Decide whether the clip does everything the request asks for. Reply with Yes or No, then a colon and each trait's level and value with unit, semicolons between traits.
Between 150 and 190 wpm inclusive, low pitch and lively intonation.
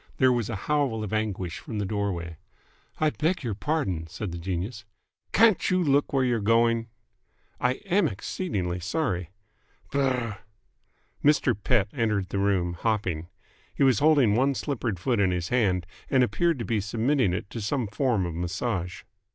Yes: average, 165 wpm; low, 110 Hz; wide, 6.0 semitones